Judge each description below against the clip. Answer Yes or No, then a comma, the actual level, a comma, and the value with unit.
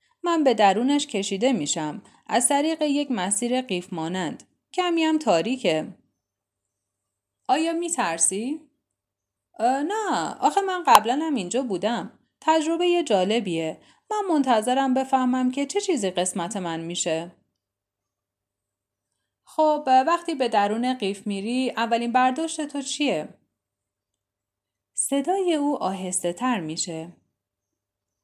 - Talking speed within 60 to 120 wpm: Yes, average, 110 wpm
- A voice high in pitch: Yes, high, 220 Hz